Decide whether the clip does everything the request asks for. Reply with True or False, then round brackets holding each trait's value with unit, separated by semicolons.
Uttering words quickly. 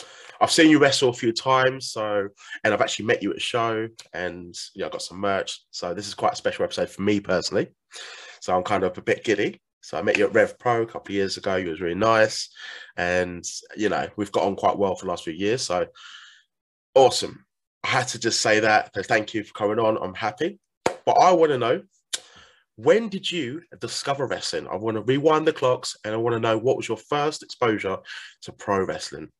True (230 wpm)